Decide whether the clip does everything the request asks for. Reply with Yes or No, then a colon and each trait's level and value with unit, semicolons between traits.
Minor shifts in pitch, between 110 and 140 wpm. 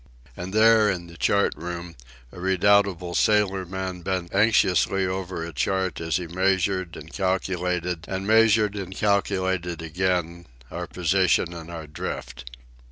Yes: narrow, 2.1 semitones; slow, 135 wpm